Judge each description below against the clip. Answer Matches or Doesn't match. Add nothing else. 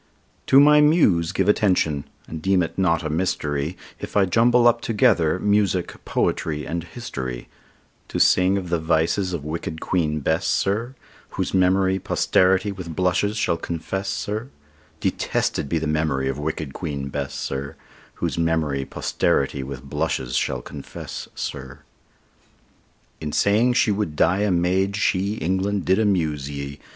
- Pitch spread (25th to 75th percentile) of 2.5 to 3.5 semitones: Doesn't match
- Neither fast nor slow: Matches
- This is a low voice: Matches